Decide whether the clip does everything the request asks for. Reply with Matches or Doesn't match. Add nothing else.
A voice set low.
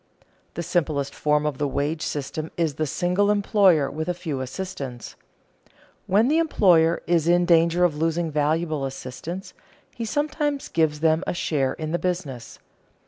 Doesn't match